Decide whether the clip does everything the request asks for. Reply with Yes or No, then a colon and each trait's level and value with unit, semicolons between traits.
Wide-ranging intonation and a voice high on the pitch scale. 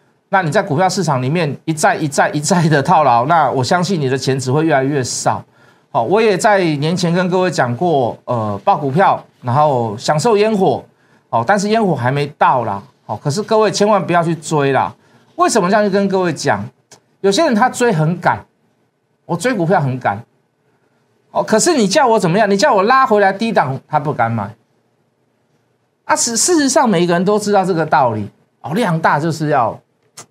No: wide, 6.6 semitones; medium, 165 Hz